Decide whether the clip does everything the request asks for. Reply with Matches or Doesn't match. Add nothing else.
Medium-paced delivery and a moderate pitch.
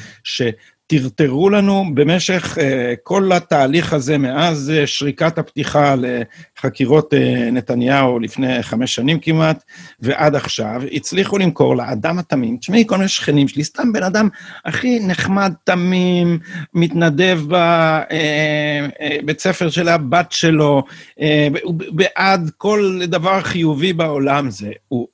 Matches